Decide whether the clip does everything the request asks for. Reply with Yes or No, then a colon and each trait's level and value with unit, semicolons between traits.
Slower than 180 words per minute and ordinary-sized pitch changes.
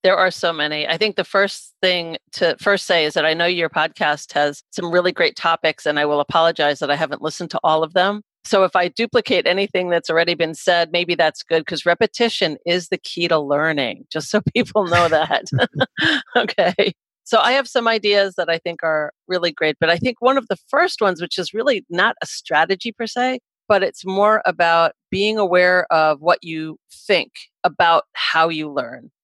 No: fast, 205 wpm; average, 3.7 semitones